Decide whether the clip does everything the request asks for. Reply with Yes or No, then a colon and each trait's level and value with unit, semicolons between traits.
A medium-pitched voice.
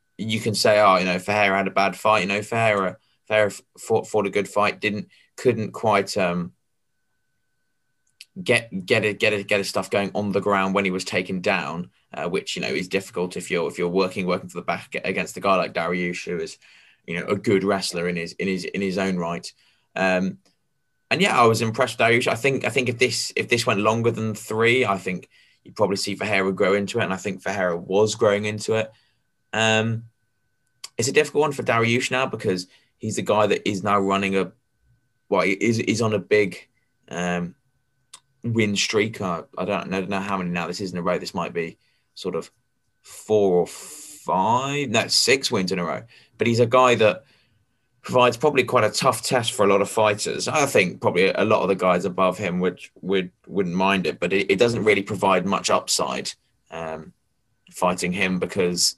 No: low, 105 Hz